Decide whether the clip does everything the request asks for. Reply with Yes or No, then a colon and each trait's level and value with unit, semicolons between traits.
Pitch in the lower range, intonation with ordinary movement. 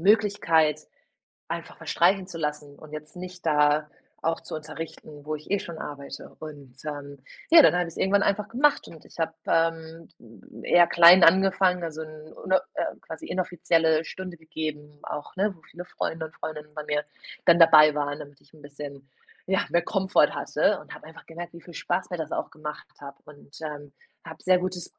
No: medium, 160 Hz; average, 3.0 semitones